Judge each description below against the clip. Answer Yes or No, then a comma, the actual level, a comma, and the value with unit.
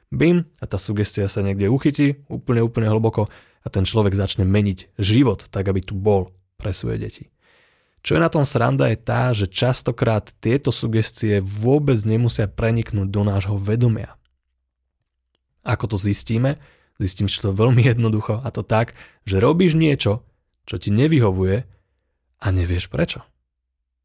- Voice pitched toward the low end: Yes, low, 110 Hz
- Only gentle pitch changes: No, average, 4.0 semitones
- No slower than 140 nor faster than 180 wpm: Yes, average, 150 wpm